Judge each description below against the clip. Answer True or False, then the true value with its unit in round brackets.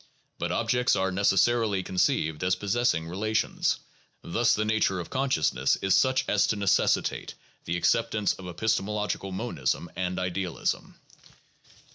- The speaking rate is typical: False (125 wpm)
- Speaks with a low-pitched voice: True (95 Hz)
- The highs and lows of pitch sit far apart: False (3.5 semitones)